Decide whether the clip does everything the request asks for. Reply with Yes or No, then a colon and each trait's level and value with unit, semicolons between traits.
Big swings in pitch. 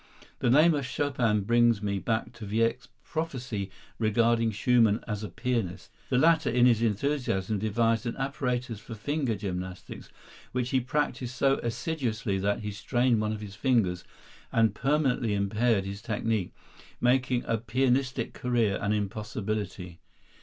No: average, 3.3 semitones